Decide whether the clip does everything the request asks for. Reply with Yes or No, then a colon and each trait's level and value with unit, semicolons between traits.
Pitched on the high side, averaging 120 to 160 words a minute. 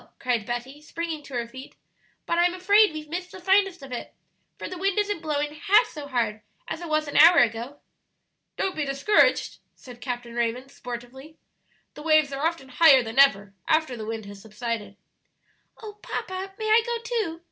No: very high, 295 Hz; average, 185 wpm